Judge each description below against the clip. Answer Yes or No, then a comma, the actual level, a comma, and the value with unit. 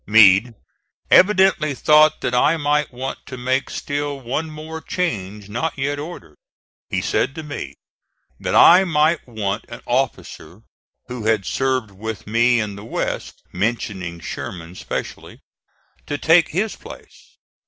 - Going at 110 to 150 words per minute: Yes, average, 140 wpm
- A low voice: Yes, low, 125 Hz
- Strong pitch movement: Yes, wide, 6.2 semitones